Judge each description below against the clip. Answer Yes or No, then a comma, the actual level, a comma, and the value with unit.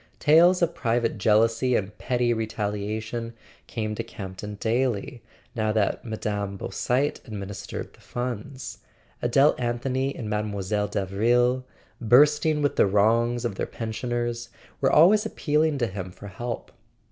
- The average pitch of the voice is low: Yes, low, 115 Hz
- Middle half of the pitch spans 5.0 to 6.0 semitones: No, average, 3.3 semitones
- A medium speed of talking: No, slow, 130 wpm